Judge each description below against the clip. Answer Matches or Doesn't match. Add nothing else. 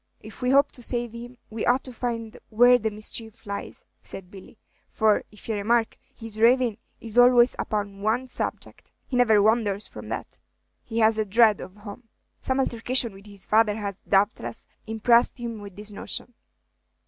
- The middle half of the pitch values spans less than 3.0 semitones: Matches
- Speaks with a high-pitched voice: Matches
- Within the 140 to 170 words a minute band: Doesn't match